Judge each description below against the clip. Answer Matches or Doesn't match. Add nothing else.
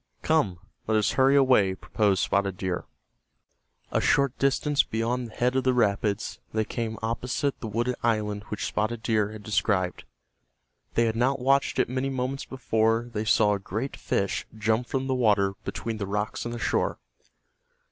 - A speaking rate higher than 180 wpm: Doesn't match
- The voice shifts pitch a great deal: Doesn't match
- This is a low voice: Matches